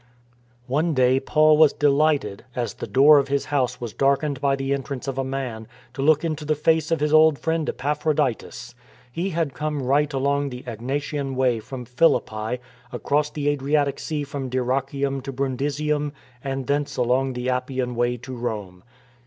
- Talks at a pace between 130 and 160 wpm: No, average, 175 wpm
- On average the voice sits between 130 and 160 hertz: Yes, low, 135 Hz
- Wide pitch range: No, average, 2.7 semitones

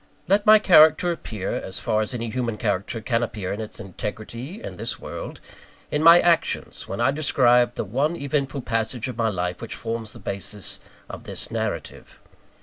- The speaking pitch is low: Yes, low, 120 Hz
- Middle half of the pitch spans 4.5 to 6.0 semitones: Yes, average, 5.3 semitones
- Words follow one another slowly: No, average, 180 wpm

